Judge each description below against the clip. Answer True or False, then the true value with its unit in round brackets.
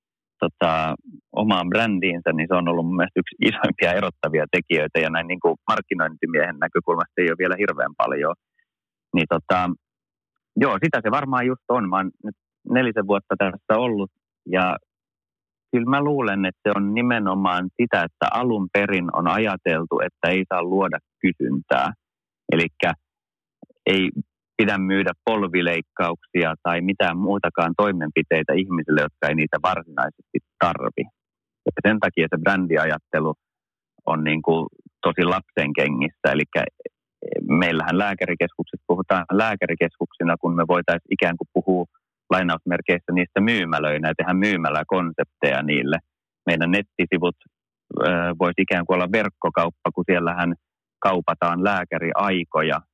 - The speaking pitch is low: True (90 Hz)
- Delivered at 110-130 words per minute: True (125 wpm)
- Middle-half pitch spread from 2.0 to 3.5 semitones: True (2.8 semitones)